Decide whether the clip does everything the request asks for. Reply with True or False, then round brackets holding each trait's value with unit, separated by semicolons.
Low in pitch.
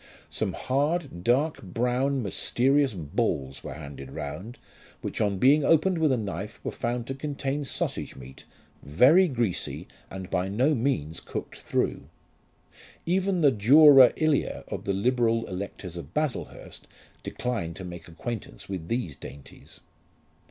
True (120 Hz)